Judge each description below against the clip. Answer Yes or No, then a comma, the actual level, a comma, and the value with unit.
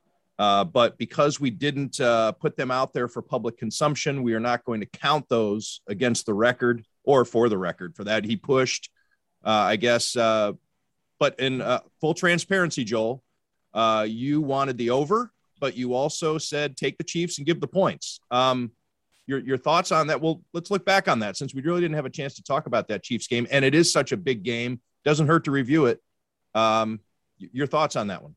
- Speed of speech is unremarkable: No, fast, 210 wpm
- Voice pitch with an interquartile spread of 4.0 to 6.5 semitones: Yes, average, 4.7 semitones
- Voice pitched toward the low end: Yes, low, 130 Hz